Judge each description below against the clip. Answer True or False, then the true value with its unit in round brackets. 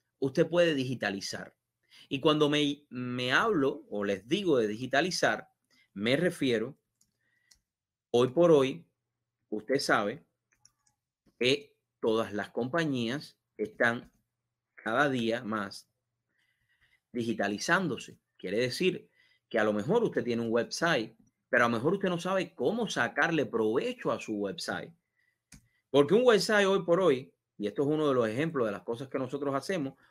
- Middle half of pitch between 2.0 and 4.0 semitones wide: False (4.6 semitones)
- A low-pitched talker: True (125 Hz)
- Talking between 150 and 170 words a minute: False (140 wpm)